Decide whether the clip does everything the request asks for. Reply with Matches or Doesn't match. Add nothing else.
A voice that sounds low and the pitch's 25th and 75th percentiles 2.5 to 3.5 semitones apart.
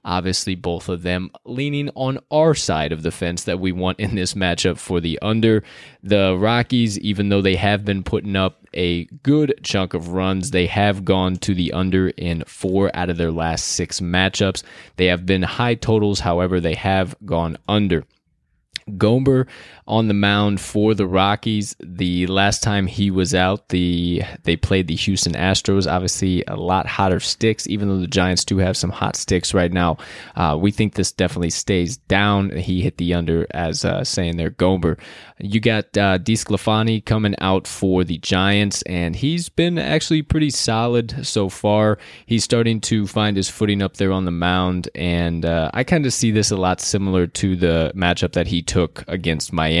Matches